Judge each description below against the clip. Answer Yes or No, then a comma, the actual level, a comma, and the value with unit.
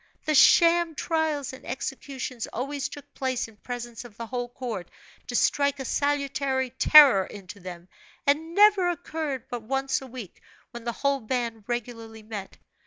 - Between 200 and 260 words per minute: No, average, 160 wpm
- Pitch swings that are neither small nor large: Yes, average, 3.6 semitones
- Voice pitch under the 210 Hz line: No, very high, 260 Hz